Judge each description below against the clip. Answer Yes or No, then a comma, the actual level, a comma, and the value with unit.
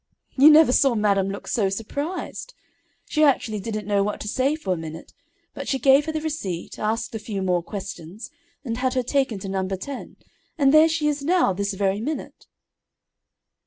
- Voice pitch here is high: Yes, high, 225 Hz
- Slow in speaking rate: No, average, 190 wpm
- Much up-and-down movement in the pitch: Yes, wide, 6.4 semitones